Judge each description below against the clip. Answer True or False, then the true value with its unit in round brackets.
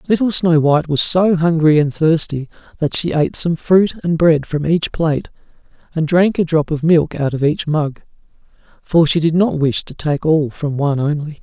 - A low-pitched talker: False (160 Hz)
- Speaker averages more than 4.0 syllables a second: True (5.0 syllables/s)